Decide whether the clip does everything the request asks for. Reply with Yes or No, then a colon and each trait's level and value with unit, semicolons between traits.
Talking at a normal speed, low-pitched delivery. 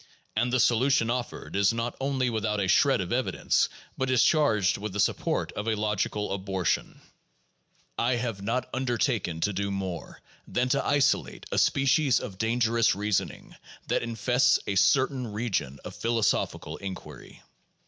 Yes: average, 150 wpm; low, 115 Hz